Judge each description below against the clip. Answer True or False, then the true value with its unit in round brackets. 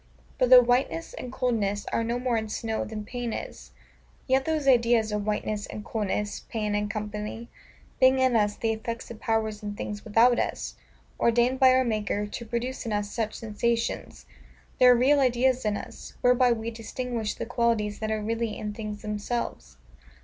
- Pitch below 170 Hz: False (225 Hz)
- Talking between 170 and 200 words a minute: True (180 wpm)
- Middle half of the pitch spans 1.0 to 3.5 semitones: True (2.7 semitones)